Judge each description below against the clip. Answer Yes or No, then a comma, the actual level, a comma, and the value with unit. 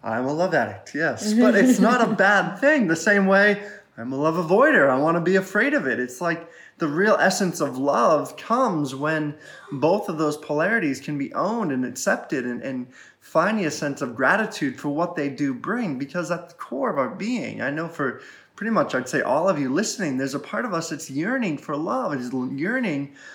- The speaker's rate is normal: No, fast, 215 wpm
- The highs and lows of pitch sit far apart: Yes, wide, 6.1 semitones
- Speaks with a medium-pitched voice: Yes, medium, 165 Hz